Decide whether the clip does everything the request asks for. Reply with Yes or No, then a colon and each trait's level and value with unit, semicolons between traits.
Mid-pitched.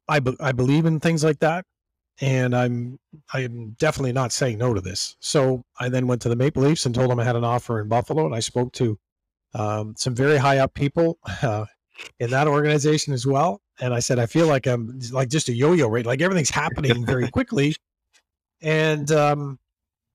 No: low, 130 Hz